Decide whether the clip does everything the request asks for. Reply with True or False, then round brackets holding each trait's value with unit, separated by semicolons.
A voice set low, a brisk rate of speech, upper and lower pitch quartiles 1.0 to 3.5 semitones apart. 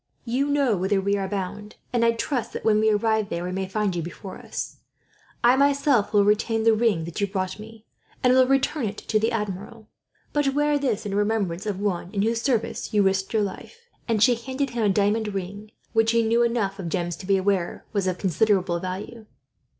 False (210 Hz; 215 wpm; 3.2 semitones)